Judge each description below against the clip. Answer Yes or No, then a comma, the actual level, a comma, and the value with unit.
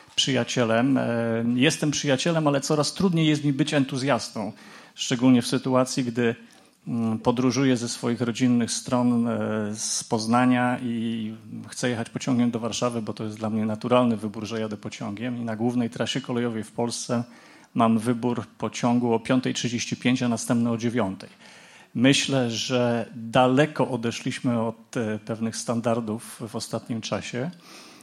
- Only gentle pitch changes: Yes, narrow, 2.1 semitones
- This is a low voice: Yes, low, 120 Hz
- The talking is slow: No, average, 135 wpm